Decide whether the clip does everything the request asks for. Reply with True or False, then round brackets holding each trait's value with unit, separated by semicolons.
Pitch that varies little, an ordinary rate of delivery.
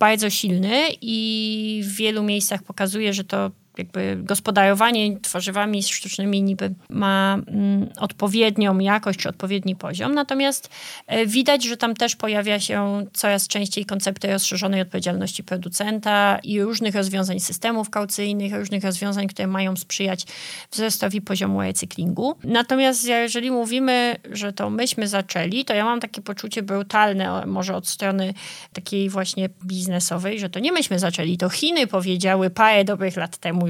True (2.3 semitones; 135 wpm)